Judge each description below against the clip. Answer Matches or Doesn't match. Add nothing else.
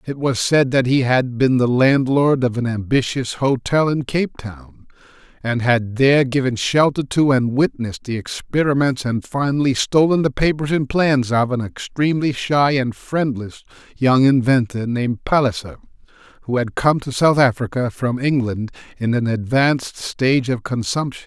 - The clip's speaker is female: Doesn't match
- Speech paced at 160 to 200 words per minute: Matches